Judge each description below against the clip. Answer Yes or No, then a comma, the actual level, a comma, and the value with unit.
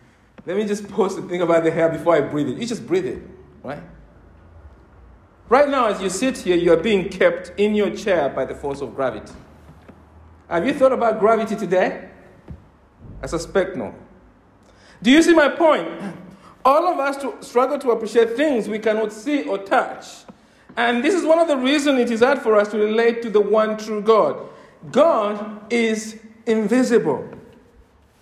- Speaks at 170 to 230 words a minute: Yes, average, 180 wpm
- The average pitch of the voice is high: Yes, high, 220 Hz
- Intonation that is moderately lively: No, wide, 5.8 semitones